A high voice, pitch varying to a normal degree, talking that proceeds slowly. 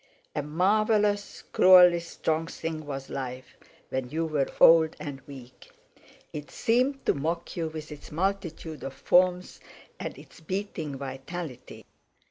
No: medium, 160 Hz; average, 4.2 semitones; slow, 130 wpm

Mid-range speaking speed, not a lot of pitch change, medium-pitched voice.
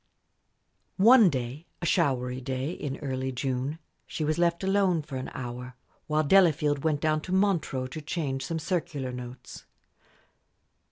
No: average, 145 wpm; average, 4.6 semitones; medium, 150 Hz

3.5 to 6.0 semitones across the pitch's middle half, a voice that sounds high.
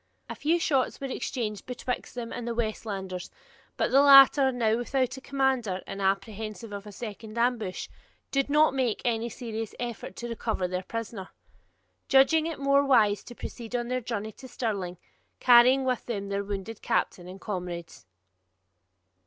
Yes: average, 4.1 semitones; high, 230 Hz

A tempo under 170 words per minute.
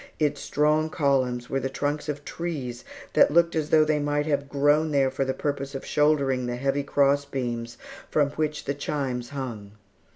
No: average, 185 wpm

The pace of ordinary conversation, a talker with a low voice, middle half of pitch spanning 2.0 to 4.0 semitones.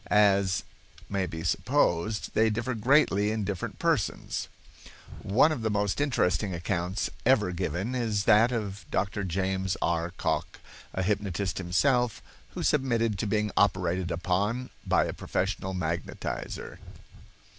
No: slow, 130 wpm; low, 100 Hz; average, 3.4 semitones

